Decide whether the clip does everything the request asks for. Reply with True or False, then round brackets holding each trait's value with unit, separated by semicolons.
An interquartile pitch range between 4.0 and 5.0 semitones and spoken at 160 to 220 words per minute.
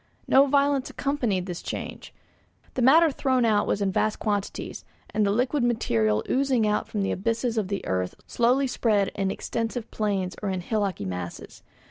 True (4.6 semitones; 170 wpm)